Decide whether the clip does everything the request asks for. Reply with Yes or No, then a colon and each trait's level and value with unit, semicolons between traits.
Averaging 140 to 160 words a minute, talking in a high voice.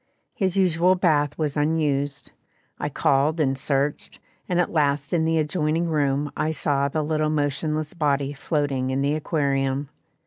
No: average, 150 wpm; medium, 150 Hz